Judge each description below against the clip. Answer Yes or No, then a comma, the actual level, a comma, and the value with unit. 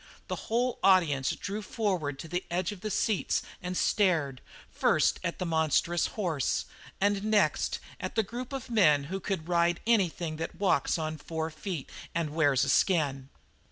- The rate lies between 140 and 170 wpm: Yes, average, 165 wpm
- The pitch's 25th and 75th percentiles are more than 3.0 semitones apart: Yes, average, 4.5 semitones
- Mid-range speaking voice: Yes, medium, 175 Hz